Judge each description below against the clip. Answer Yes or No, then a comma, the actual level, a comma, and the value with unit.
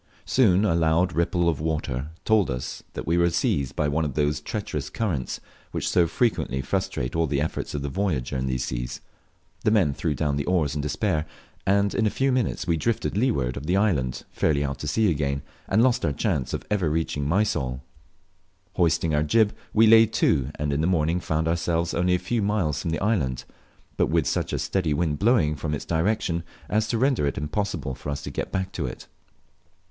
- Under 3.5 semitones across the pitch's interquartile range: No, wide, 5.4 semitones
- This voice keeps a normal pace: No, fast, 210 wpm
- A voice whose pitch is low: Yes, very low, 80 Hz